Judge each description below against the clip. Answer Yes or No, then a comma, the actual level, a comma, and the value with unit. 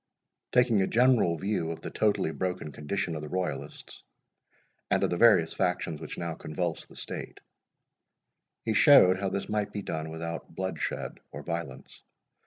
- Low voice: Yes, very low, 90 Hz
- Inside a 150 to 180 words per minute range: Yes, average, 160 wpm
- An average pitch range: Yes, average, 3.8 semitones